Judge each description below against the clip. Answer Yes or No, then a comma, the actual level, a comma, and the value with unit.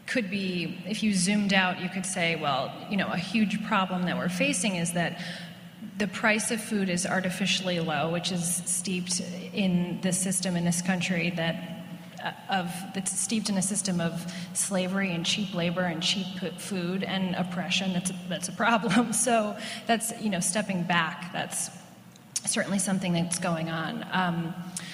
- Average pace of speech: Yes, average, 175 wpm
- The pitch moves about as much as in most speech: No, narrow, 1.9 semitones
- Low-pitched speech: No, medium, 185 Hz